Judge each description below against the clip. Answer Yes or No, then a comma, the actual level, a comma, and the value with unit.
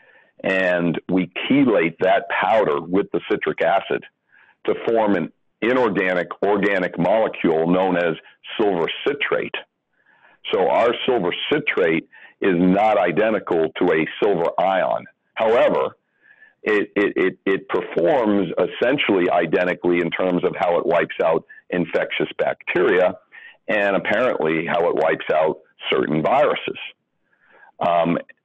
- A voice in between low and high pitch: No, very low, 95 Hz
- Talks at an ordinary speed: No, slow, 120 wpm